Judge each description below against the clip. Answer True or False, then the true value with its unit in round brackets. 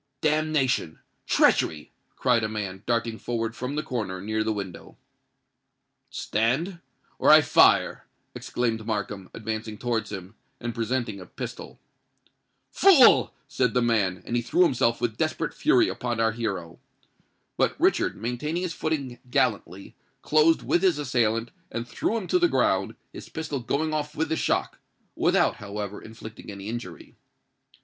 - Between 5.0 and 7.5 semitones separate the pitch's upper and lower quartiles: True (5.5 semitones)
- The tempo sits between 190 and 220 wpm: False (140 wpm)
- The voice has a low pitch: True (115 Hz)